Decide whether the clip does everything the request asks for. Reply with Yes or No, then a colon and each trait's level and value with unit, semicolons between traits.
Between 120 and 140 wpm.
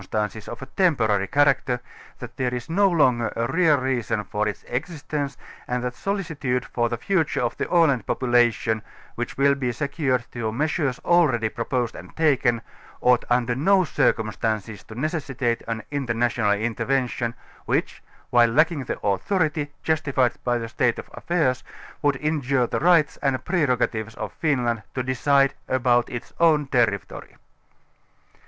No: average, 150 wpm